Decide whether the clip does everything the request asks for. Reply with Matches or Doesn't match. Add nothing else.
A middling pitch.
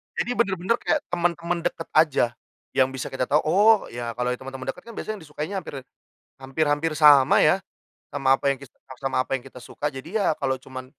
Matches